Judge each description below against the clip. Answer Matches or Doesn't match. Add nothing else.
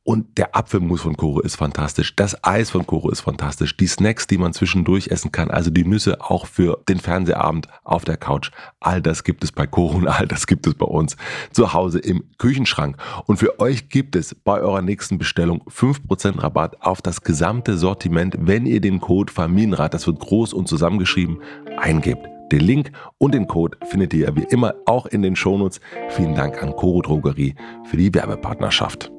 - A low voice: Matches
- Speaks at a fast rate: Matches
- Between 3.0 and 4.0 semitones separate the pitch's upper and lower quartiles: Matches